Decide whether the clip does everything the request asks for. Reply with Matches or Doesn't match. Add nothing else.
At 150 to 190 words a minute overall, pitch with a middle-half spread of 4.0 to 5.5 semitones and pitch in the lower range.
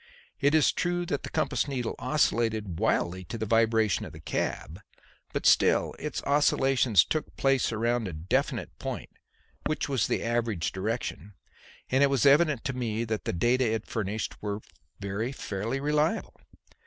Matches